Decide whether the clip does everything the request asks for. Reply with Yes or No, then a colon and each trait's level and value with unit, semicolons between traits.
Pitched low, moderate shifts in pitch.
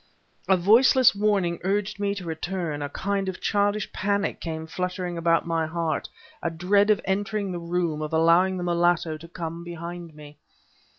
No: medium, 175 Hz; average, 3.2 semitones